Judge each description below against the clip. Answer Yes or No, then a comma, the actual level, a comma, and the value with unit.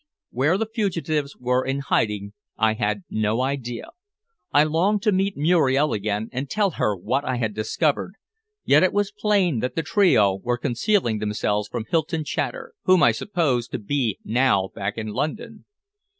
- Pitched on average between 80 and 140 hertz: Yes, low, 135 Hz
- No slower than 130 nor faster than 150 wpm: No, average, 165 wpm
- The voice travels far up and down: Yes, wide, 8.3 semitones